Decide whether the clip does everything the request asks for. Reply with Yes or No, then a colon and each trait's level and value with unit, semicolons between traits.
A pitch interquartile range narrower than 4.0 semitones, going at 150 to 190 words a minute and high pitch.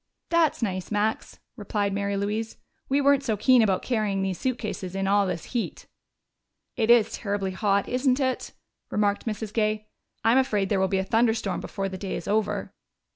Yes: average, 2.9 semitones; average, 180 wpm; high, 210 Hz